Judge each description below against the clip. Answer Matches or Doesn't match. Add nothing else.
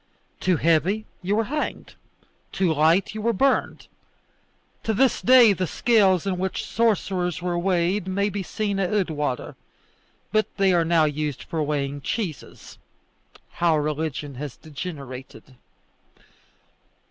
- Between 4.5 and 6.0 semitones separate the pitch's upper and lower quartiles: Matches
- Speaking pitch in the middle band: Matches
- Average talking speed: Doesn't match